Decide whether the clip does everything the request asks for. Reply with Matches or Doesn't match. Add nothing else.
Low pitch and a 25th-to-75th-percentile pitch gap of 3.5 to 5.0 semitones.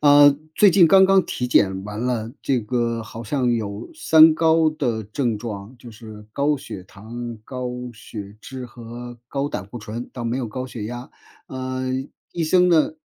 Matches